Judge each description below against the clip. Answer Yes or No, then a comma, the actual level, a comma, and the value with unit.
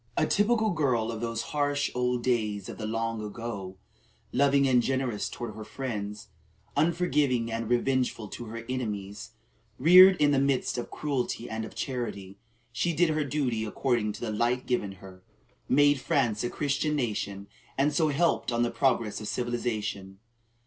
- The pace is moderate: Yes, average, 165 wpm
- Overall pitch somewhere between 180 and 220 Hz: No, low, 120 Hz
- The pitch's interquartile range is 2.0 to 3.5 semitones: No, average, 4.5 semitones